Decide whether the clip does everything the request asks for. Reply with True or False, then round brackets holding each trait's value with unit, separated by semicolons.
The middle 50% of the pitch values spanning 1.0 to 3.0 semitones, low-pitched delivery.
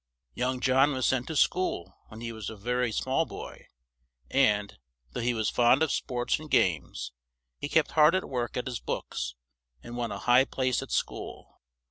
True (2.7 semitones; 125 Hz)